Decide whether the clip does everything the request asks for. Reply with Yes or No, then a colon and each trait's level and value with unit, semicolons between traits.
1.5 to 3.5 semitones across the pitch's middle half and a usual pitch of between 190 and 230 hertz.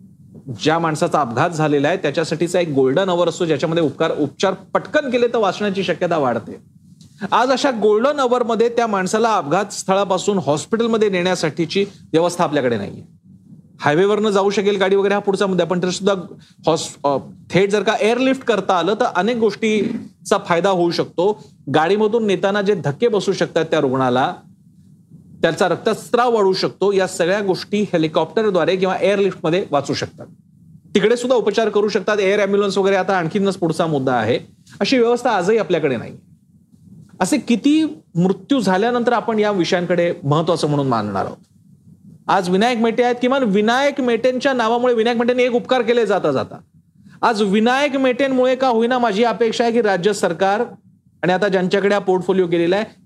No: average, 4.8 semitones; high, 195 Hz